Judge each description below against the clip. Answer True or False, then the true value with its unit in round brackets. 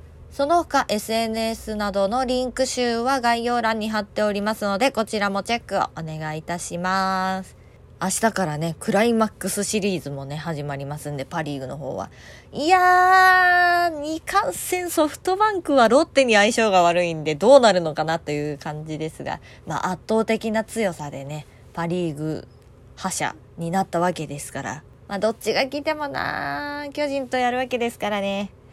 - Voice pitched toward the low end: False (205 Hz)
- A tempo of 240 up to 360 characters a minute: True (340 characters per minute)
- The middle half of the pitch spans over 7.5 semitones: True (8.1 semitones)